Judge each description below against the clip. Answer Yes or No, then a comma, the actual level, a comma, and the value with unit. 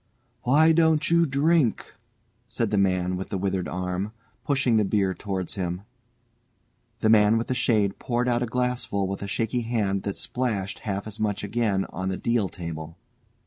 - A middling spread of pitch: Yes, average, 4.3 semitones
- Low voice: Yes, low, 105 Hz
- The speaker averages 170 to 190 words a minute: Yes, average, 175 wpm